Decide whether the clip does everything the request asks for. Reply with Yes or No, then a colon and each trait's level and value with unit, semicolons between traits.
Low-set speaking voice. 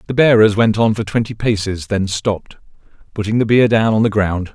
Yes: low, 105 Hz